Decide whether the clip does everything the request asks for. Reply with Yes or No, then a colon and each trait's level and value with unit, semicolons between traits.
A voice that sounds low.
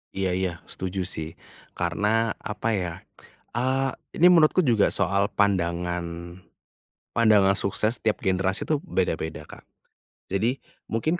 Yes: low, 100 Hz